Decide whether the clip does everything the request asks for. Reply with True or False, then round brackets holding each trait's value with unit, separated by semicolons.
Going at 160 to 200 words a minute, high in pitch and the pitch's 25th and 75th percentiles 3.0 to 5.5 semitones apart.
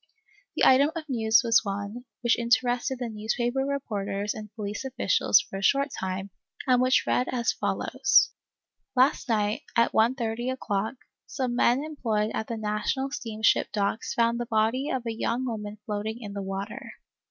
True (175 wpm; 230 Hz; 3.3 semitones)